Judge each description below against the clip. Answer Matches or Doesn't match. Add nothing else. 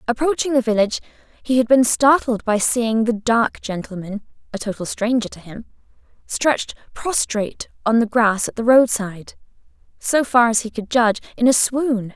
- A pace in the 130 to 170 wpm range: Matches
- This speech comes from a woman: Matches